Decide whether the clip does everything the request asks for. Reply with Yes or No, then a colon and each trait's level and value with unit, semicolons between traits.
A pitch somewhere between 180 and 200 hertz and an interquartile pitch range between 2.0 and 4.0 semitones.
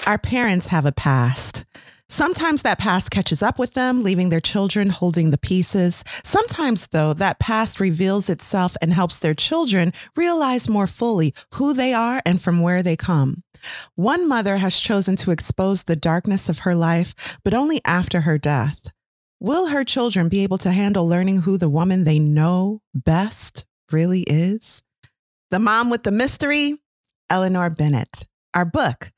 No: medium, 185 Hz; average, 4.7 semitones